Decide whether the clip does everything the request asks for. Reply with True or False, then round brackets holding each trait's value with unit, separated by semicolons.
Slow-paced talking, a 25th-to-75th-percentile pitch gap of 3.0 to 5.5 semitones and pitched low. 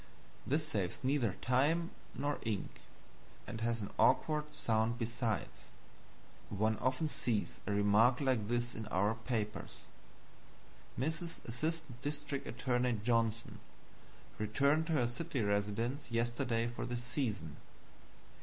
True (115 wpm; 4.1 semitones; 120 Hz)